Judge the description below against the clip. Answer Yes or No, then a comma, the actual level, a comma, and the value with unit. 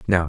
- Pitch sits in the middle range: No, very low, 90 Hz